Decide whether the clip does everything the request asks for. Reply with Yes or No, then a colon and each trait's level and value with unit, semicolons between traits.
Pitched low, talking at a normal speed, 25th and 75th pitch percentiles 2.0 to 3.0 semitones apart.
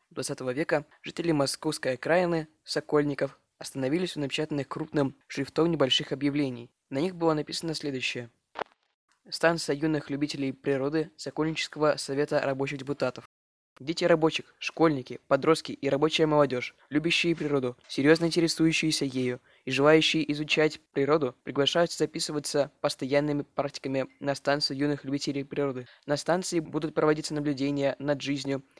No: medium, 145 Hz; average, 120 wpm; narrow, 2.4 semitones